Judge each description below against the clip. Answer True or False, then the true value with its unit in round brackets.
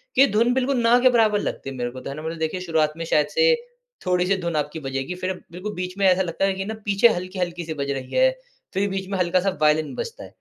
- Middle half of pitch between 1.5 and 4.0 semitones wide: False (4.4 semitones)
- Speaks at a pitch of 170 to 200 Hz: True (185 Hz)